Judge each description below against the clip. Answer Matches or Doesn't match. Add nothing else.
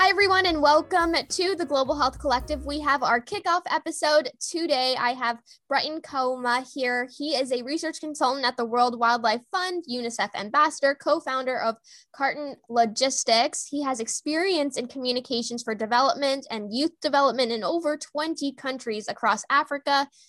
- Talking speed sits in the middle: Matches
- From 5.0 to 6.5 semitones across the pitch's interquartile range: Doesn't match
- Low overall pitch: Doesn't match